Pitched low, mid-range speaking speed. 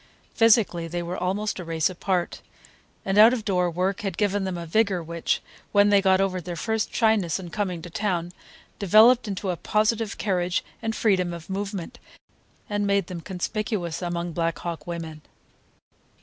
No: high, 190 Hz; average, 170 wpm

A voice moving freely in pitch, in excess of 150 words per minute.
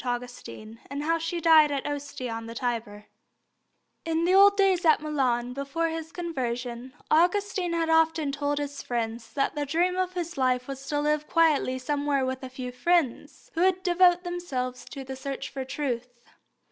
No: average, 4.7 semitones; average, 175 wpm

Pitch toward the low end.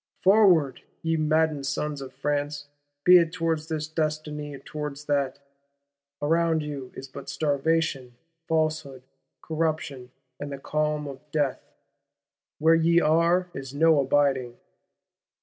No: medium, 150 Hz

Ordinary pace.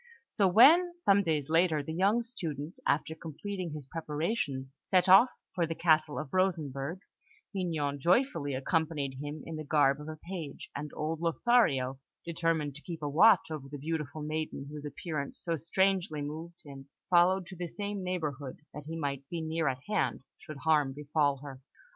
Yes: average, 170 wpm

